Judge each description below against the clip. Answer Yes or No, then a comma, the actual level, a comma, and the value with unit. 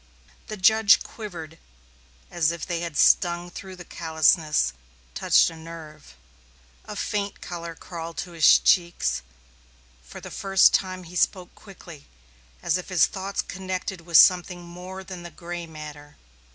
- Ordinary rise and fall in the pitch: No, narrow, 2.3 semitones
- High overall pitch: No, medium, 175 Hz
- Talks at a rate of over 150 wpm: No, average, 140 wpm